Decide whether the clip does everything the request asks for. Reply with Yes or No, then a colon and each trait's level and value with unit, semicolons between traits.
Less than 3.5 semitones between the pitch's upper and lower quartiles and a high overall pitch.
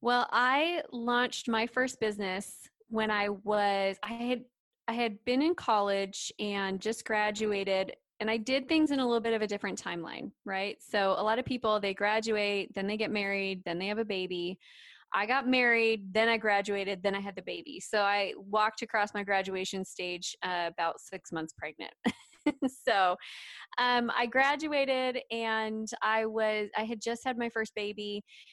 Yes: average, 3.1 semitones; high, 215 Hz